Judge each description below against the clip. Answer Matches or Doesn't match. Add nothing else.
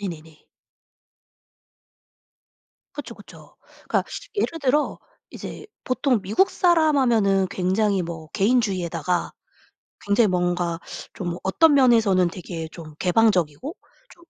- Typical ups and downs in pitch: Doesn't match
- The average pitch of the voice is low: Doesn't match